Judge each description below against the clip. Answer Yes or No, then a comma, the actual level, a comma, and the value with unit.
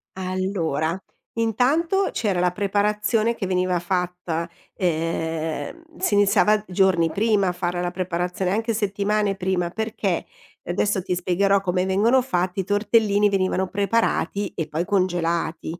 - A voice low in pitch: No, high, 190 Hz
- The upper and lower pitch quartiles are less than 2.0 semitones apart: No, average, 2.7 semitones